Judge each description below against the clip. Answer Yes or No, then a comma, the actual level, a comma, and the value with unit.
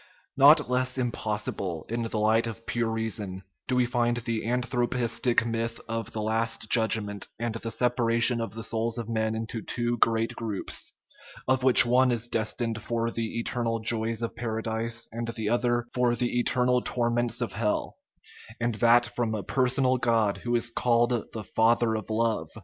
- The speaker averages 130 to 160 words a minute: No, average, 175 wpm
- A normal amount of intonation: No, narrow, 1.3 semitones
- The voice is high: No, low, 115 Hz